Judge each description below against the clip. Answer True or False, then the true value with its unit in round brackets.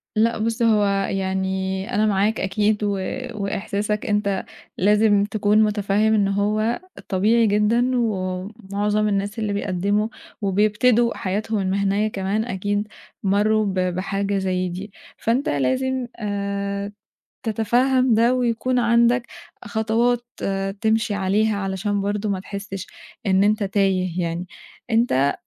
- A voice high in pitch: True (205 Hz)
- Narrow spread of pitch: True (2.1 semitones)